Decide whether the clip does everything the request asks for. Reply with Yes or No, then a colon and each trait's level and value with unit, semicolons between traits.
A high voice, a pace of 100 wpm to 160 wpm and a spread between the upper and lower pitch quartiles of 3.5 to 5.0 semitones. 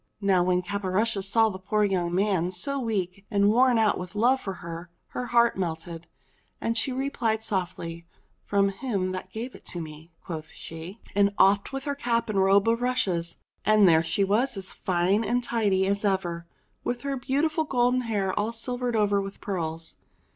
No: high, 200 Hz; average, 175 wpm; average, 4.2 semitones